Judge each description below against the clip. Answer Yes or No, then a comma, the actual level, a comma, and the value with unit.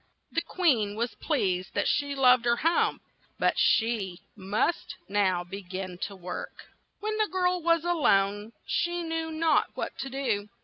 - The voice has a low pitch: No, high, 240 Hz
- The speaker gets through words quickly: No, average, 170 wpm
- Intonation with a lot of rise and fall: Yes, wide, 8.7 semitones